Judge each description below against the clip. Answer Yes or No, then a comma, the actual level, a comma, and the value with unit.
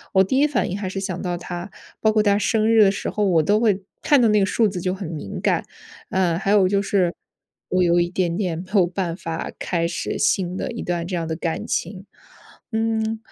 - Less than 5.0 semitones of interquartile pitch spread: Yes, average, 3.3 semitones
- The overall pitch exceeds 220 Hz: No, high, 190 Hz